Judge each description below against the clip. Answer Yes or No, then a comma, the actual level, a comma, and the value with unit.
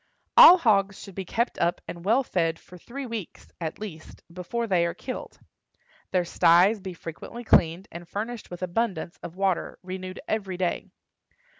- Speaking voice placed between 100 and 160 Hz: No, medium, 185 Hz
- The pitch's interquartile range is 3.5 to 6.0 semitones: Yes, average, 4.2 semitones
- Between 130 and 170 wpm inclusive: Yes, average, 165 wpm